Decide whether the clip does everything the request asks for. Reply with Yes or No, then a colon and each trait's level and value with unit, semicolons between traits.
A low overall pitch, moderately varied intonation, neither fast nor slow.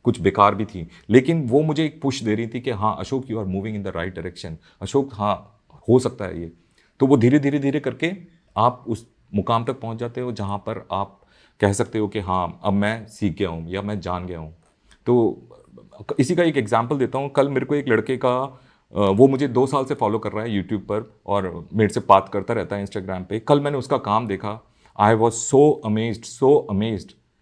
No: low, 110 Hz; average, 4.5 semitones; fast, 225 wpm